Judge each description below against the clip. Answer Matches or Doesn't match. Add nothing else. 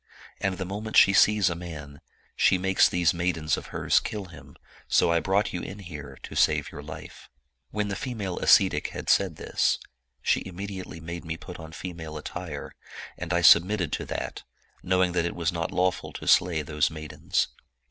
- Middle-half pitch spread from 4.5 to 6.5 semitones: Doesn't match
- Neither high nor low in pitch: Doesn't match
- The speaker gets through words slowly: Doesn't match